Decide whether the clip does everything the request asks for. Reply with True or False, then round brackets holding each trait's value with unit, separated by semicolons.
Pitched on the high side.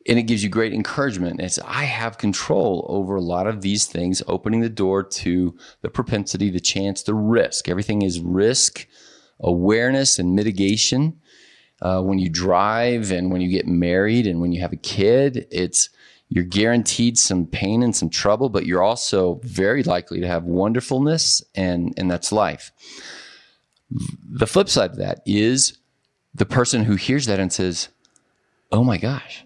False (100 Hz)